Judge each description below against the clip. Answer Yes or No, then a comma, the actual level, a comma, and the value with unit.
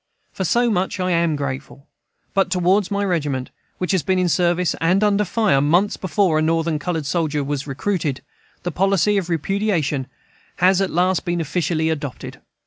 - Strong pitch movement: No, average, 3.8 semitones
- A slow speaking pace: No, average, 170 wpm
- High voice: No, medium, 175 Hz